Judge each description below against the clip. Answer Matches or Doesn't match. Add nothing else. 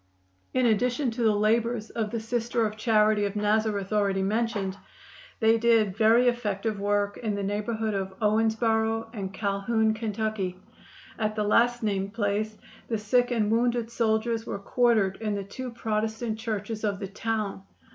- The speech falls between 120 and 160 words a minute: Matches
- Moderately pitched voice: Doesn't match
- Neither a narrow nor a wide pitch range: Doesn't match